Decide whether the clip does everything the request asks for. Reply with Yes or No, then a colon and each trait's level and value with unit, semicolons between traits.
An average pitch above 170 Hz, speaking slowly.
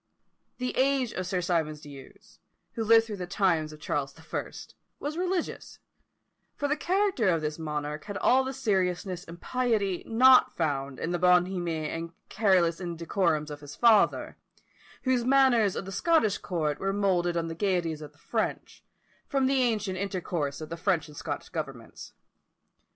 No: medium, 185 Hz; average, 165 wpm